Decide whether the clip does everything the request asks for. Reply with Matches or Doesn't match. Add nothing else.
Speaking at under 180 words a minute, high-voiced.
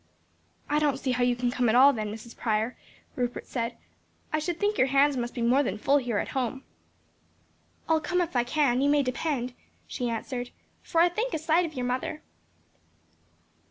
Doesn't match